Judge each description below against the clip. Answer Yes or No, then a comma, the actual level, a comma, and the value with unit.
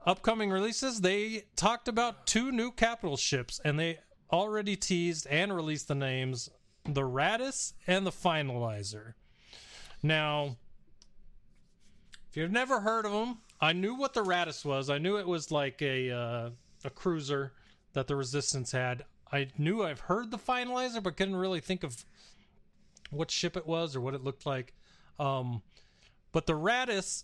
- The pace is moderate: Yes, average, 155 wpm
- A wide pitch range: Yes, wide, 7.0 semitones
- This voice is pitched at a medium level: Yes, medium, 165 Hz